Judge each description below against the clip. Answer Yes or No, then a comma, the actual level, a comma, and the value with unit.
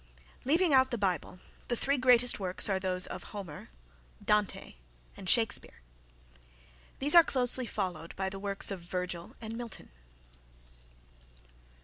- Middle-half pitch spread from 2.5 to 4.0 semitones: No, average, 5.0 semitones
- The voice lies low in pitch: No, high, 205 Hz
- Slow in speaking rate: Yes, slow, 130 wpm